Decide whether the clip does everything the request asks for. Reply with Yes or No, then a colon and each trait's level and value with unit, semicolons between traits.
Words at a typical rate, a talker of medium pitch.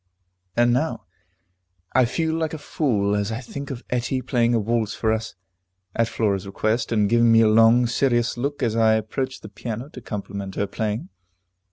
No: average, 185 wpm; low, 115 Hz